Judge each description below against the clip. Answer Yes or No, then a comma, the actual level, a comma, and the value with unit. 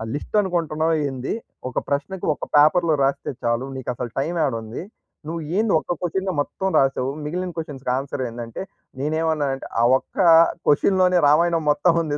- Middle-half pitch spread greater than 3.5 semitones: Yes, average, 4.3 semitones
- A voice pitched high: No, medium, 150 Hz